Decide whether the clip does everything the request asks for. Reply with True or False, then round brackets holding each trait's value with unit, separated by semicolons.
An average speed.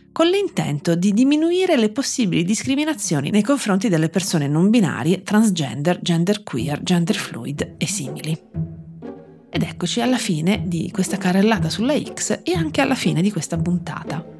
True (150 wpm)